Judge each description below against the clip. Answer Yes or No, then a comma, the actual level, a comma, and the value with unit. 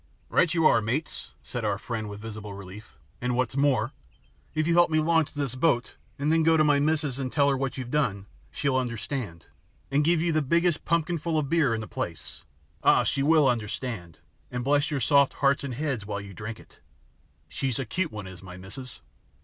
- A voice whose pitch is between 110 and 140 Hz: Yes, low, 135 Hz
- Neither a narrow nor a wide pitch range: No, wide, 5.8 semitones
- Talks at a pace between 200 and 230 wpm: Yes, fast, 205 wpm